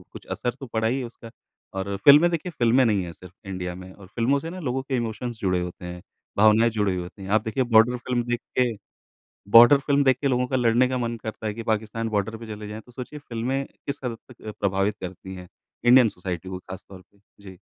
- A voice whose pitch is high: No, low, 115 Hz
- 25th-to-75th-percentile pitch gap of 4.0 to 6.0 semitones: Yes, average, 4.3 semitones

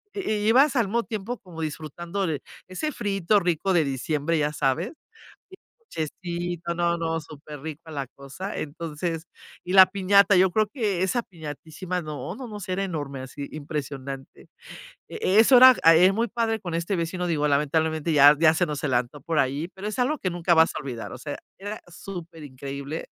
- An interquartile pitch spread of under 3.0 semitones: No, average, 4.7 semitones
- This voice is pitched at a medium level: Yes, medium, 170 Hz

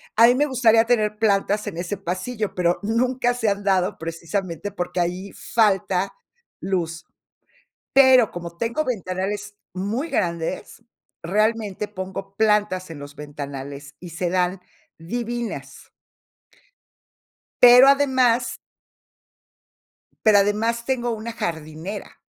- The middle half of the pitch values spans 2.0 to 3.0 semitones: No, average, 4.6 semitones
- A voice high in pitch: Yes, high, 205 Hz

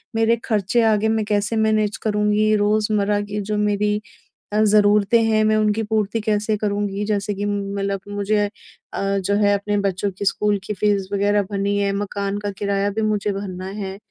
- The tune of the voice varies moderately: No, narrow, 1.0 semitones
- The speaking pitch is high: Yes, high, 205 Hz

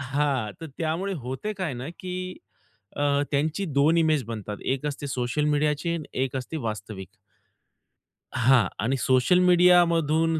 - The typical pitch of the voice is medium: Yes, medium, 145 Hz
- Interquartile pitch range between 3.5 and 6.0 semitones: Yes, average, 4.2 semitones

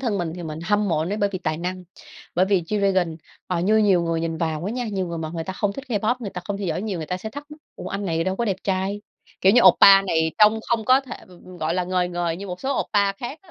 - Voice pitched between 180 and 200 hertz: Yes, high, 190 Hz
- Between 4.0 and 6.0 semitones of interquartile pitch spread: No, average, 3.5 semitones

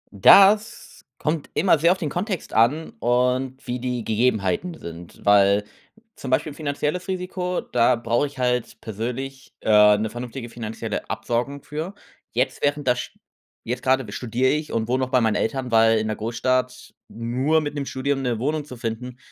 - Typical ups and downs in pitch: Yes, average, 4.0 semitones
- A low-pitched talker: Yes, low, 125 Hz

